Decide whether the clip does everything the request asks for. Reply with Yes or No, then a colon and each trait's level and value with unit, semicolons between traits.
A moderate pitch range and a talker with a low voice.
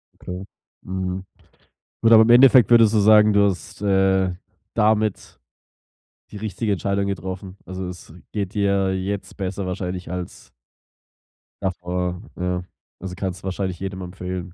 No: narrow, 2.0 semitones; very low, 95 Hz